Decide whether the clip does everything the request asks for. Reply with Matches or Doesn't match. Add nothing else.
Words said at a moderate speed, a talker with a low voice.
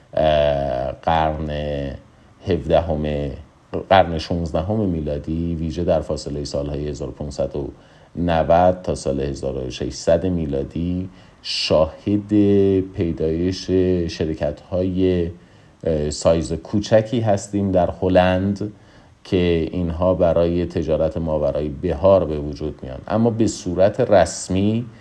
Doesn't match